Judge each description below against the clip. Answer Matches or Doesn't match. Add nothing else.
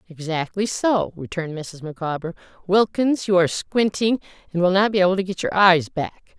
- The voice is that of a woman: Matches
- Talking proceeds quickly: Doesn't match